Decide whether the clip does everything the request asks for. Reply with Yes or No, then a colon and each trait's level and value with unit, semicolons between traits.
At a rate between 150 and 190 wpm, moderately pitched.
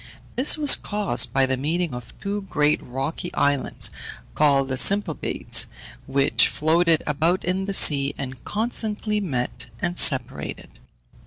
No: slow, 135 wpm; medium, 155 Hz